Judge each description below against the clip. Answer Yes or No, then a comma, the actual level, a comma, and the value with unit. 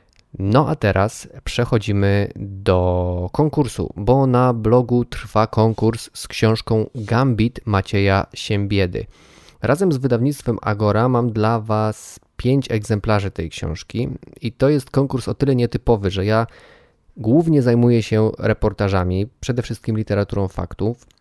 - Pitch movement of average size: Yes, average, 3.5 semitones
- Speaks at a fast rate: No, average, 125 wpm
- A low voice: Yes, low, 110 Hz